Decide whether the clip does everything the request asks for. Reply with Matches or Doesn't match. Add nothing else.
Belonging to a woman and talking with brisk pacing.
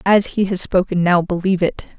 Matches